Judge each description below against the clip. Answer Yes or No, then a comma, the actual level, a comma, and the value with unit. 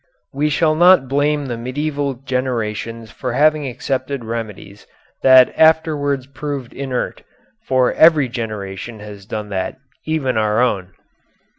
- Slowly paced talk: Yes, slow, 125 wpm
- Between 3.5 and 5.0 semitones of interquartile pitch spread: Yes, average, 4.3 semitones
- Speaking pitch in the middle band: No, low, 130 Hz